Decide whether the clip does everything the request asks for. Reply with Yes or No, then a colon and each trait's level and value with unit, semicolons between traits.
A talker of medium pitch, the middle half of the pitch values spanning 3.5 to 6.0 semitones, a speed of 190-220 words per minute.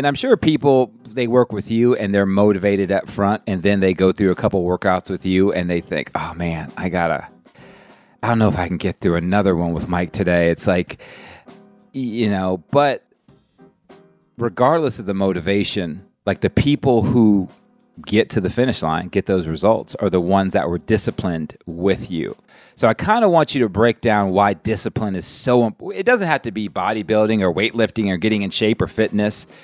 No: low, 100 Hz; average, 3.8 semitones; average, 200 wpm